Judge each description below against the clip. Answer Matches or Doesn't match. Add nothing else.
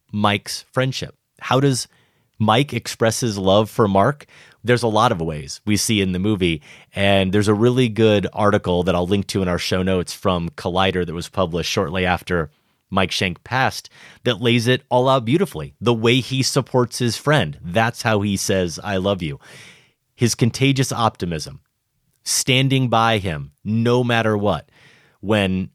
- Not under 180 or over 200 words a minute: Doesn't match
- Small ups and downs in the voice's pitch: Doesn't match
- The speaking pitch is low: Matches